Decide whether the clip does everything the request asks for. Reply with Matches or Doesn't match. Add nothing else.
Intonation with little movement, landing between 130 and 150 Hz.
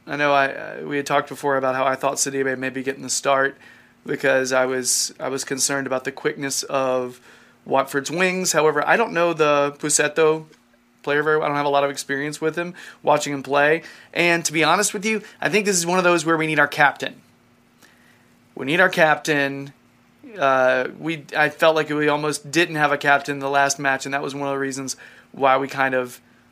Matches